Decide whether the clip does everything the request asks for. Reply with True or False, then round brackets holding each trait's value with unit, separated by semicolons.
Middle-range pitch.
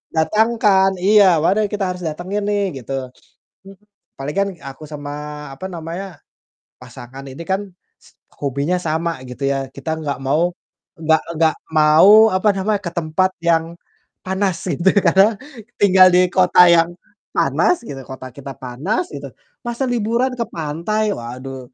True (170 Hz)